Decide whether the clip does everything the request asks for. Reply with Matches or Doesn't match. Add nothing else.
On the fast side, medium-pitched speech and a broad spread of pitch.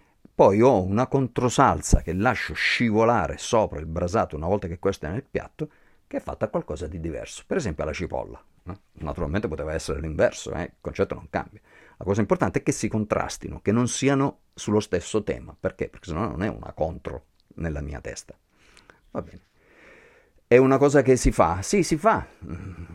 Doesn't match